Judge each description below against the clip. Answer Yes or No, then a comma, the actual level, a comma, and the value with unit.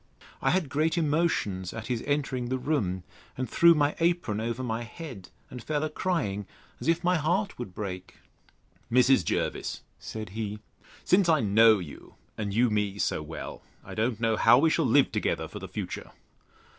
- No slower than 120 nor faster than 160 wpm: No, average, 180 wpm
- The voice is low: Yes, low, 125 Hz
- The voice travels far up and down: Yes, wide, 6.7 semitones